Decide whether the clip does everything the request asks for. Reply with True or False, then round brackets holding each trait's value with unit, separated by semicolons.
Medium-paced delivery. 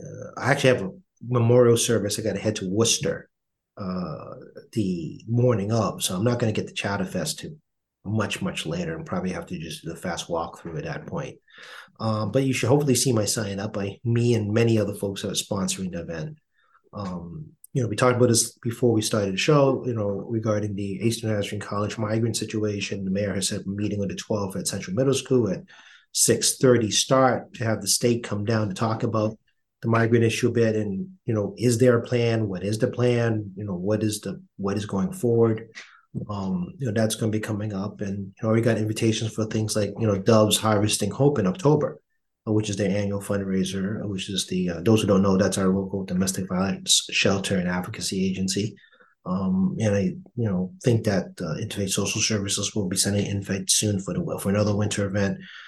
False (220 wpm)